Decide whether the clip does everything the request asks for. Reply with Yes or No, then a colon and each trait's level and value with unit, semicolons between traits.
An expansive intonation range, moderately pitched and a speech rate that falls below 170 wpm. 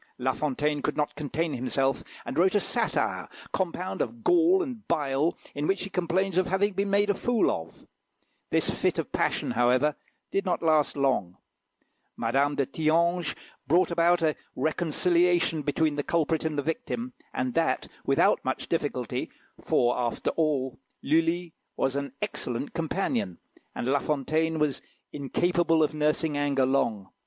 No: average, 4.0 semitones; medium, 155 Hz; average, 155 wpm